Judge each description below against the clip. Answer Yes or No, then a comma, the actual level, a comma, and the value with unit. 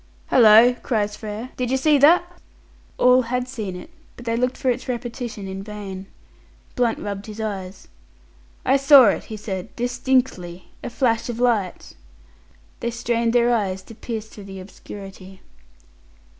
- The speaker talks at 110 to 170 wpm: Yes, average, 155 wpm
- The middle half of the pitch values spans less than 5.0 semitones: Yes, average, 3.7 semitones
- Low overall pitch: No, high, 230 Hz